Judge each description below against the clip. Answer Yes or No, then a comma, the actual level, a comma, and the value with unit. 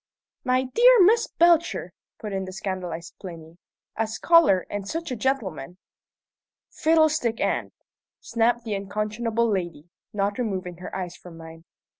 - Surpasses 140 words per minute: No, slow, 135 wpm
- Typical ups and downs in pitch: No, wide, 5.9 semitones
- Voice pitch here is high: Yes, high, 210 Hz